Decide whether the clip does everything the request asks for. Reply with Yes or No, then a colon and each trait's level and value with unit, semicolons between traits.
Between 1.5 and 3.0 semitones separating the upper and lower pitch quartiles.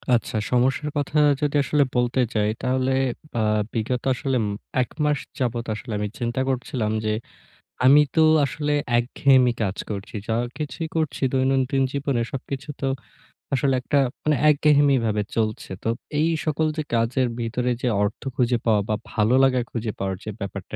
No: average, 3.6 semitones